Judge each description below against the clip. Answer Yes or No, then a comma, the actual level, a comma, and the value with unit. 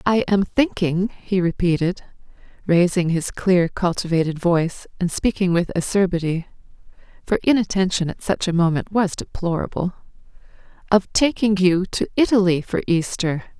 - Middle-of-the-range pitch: Yes, medium, 180 Hz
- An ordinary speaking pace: No, slow, 130 wpm